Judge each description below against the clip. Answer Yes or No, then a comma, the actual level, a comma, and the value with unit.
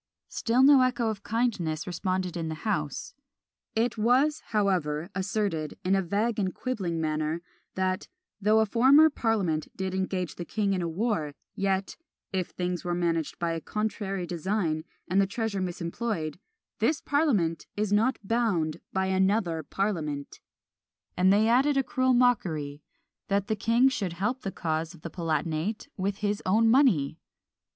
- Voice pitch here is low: No, high, 190 Hz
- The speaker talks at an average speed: Yes, average, 155 wpm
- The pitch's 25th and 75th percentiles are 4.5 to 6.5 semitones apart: Yes, average, 4.9 semitones